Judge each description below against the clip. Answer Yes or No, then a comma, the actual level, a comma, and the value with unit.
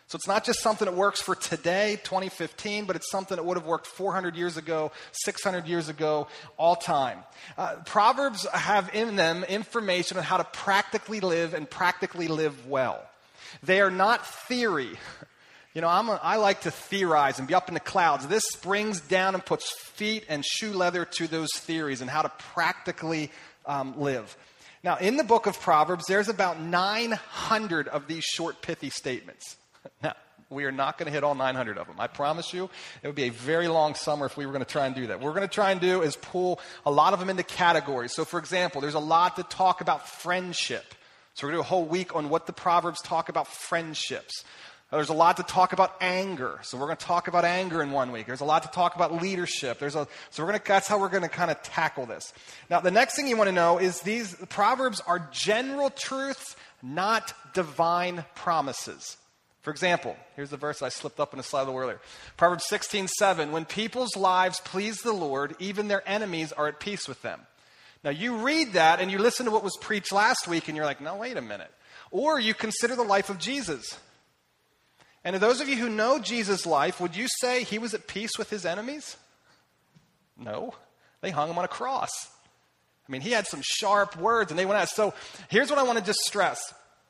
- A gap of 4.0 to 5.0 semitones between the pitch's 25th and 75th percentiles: Yes, average, 4.4 semitones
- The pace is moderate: No, fast, 220 wpm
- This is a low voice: No, medium, 180 Hz